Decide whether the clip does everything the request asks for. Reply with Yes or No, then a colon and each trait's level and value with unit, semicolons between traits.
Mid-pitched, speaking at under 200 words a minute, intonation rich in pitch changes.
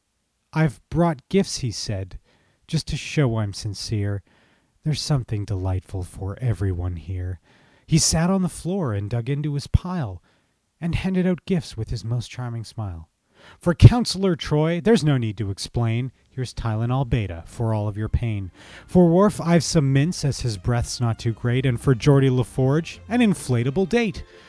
No: low, 125 Hz; average, 170 wpm; wide, 7.1 semitones